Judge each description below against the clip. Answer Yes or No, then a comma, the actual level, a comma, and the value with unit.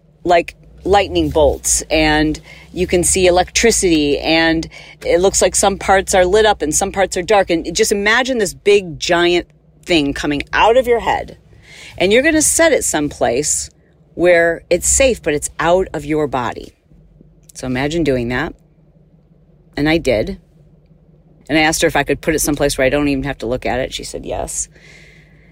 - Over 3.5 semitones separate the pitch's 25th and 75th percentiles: No, average, 2.9 semitones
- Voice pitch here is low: No, medium, 165 Hz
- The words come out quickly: No, average, 185 wpm